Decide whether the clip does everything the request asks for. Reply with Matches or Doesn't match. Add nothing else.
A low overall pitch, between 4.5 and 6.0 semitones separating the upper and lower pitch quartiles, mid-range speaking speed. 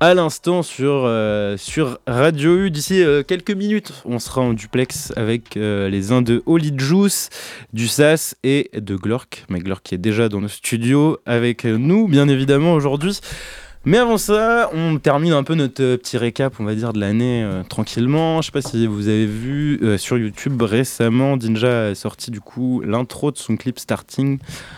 Matches